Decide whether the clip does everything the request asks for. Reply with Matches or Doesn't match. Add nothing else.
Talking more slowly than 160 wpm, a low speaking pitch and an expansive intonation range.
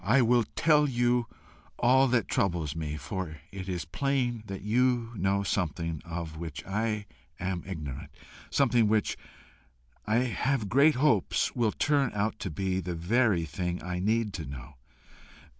Matches